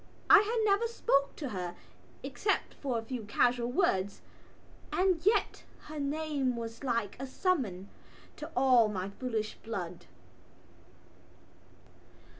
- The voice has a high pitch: Yes, very high, 250 Hz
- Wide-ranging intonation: Yes, wide, 6.7 semitones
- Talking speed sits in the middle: No, slow, 120 wpm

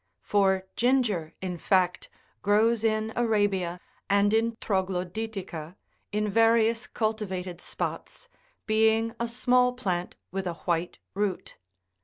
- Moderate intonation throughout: Yes, average, 3.4 semitones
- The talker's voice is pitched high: Yes, high, 210 Hz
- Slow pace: Yes, slow, 110 wpm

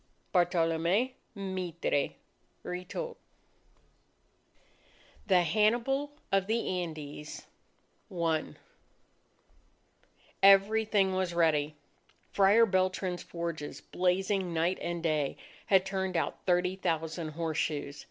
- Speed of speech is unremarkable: No, slow, 85 wpm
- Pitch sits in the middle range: Yes, medium, 180 Hz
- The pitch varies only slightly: No, average, 3.0 semitones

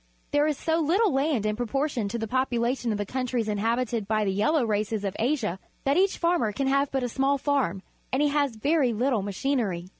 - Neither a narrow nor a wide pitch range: Yes, average, 4.8 semitones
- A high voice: Yes, very high, 250 Hz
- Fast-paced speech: Yes, fast, 210 wpm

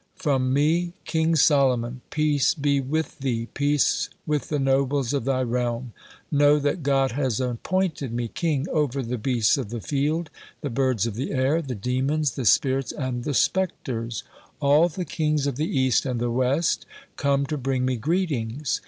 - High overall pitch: No, low, 135 Hz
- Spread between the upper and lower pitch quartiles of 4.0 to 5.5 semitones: No, average, 3.0 semitones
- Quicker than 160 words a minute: Yes, average, 170 wpm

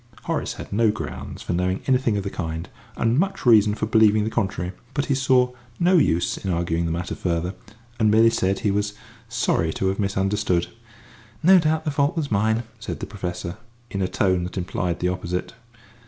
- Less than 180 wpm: No, average, 195 wpm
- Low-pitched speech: Yes, low, 105 Hz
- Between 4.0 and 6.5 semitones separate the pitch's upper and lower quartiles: Yes, average, 4.4 semitones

